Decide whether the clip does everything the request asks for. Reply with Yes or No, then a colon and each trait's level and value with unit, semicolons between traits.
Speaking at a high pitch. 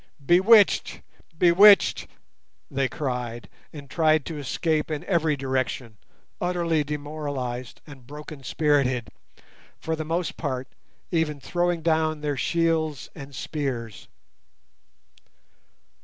No: medium, 150 Hz